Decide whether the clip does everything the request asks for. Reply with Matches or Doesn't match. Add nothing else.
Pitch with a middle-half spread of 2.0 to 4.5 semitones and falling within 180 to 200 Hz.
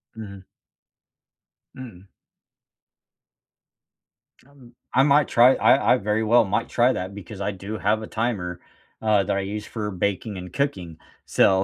Doesn't match